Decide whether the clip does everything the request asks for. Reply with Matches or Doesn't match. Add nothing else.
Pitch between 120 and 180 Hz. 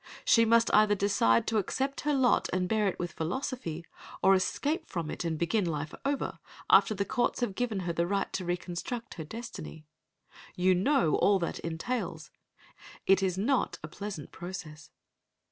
Doesn't match